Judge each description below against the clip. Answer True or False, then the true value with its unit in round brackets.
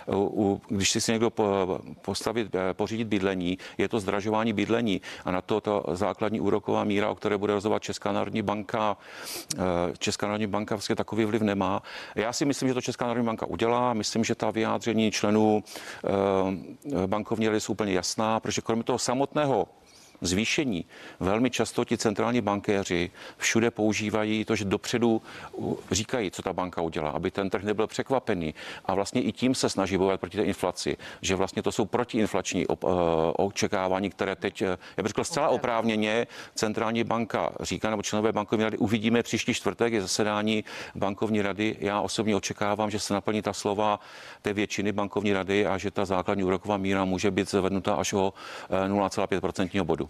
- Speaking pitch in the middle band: False (105 Hz)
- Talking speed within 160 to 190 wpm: True (165 wpm)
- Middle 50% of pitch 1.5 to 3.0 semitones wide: True (2.4 semitones)